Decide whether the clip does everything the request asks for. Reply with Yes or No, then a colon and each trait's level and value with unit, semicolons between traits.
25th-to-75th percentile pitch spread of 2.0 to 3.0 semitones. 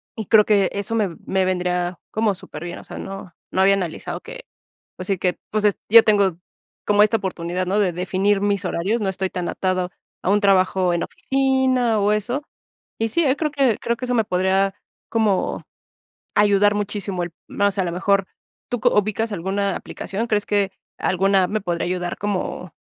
Yes: narrow, 2.4 semitones